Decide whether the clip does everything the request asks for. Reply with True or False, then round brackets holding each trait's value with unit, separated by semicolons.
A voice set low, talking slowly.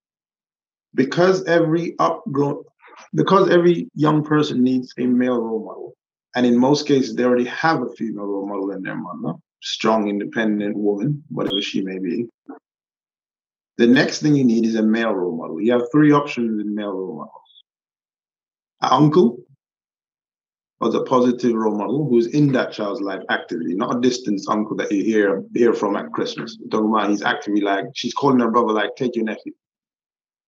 False (120 Hz; 170 wpm)